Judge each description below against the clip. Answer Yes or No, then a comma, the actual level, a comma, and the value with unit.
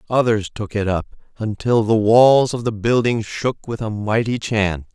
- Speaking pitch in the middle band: No, low, 110 Hz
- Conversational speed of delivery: Yes, average, 180 wpm